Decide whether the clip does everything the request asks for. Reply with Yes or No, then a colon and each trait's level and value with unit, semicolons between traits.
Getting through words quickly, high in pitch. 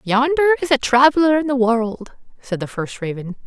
No: average, 190 wpm; very high, 250 Hz